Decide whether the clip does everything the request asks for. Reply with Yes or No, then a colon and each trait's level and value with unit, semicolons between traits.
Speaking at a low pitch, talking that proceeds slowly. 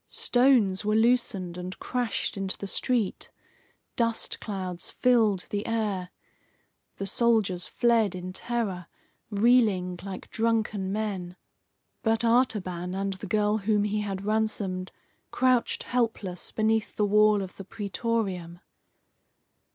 No: high, 210 Hz; slow, 120 wpm